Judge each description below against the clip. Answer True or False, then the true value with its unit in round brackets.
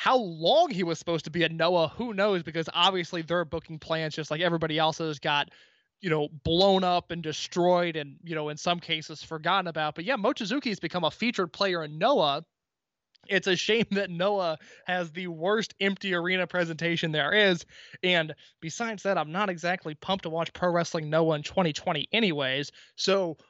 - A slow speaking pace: False (185 wpm)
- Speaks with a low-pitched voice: False (175 Hz)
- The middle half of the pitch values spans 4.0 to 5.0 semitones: False (3.2 semitones)